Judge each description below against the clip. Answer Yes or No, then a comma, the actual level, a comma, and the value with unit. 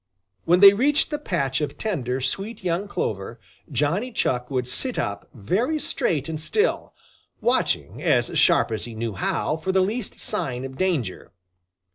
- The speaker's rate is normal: Yes, average, 160 wpm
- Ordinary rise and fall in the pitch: No, wide, 8.4 semitones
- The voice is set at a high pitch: No, medium, 160 Hz